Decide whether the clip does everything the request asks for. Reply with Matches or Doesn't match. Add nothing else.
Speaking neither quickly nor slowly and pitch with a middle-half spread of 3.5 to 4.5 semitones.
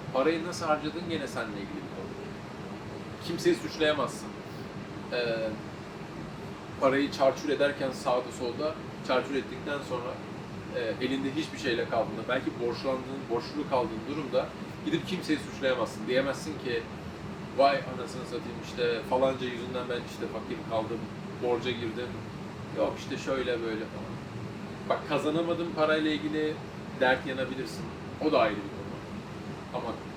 Matches